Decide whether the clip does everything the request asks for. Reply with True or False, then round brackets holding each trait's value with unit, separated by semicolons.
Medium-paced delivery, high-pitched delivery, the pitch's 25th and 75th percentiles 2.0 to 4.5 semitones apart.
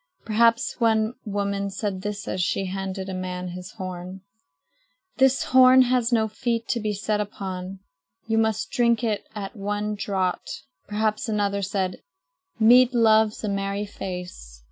True (145 wpm; 205 Hz; 2.6 semitones)